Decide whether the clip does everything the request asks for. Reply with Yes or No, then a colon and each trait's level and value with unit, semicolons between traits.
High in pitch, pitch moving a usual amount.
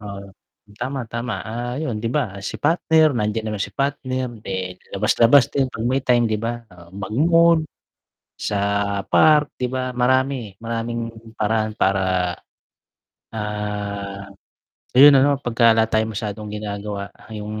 No: low, 115 Hz; average, 3.7 semitones